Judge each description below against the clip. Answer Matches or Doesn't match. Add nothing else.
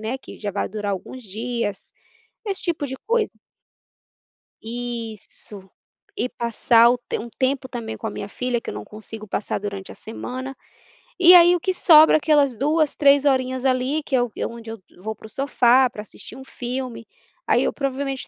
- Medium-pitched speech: Doesn't match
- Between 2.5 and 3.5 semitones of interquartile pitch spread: Doesn't match